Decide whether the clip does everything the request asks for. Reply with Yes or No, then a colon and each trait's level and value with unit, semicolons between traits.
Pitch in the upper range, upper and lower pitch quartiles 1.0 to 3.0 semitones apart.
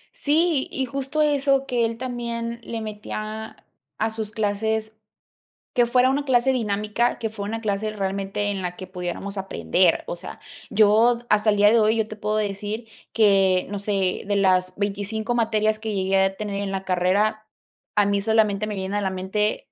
Yes: high, 215 Hz; narrow, 2.5 semitones